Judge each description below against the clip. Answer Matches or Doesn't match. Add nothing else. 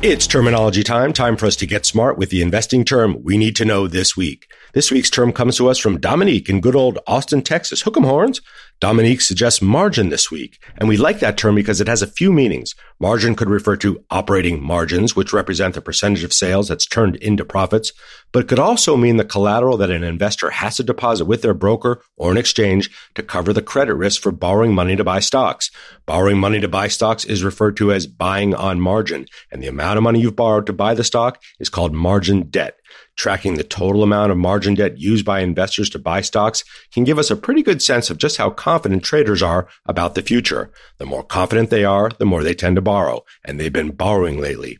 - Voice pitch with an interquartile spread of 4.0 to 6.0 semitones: Doesn't match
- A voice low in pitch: Matches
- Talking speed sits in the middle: Doesn't match